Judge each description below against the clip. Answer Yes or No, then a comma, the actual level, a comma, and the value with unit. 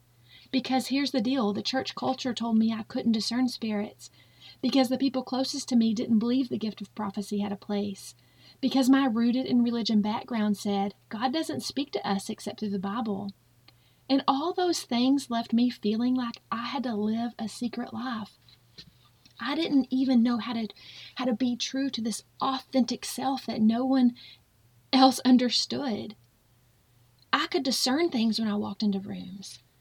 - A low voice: No, high, 230 Hz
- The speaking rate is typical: Yes, average, 175 wpm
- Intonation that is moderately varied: Yes, average, 4.3 semitones